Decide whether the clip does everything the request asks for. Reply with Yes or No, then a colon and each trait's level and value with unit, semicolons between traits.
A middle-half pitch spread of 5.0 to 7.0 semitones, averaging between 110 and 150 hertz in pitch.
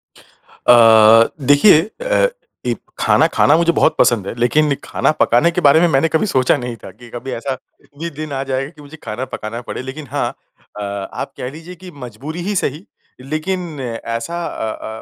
Yes: average, 5.3 semitones; low, 135 Hz